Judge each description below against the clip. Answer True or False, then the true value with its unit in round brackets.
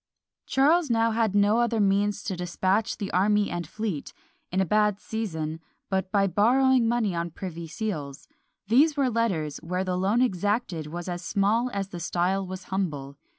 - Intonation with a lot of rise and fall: False (4.2 semitones)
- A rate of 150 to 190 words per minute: True (170 wpm)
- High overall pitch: True (195 Hz)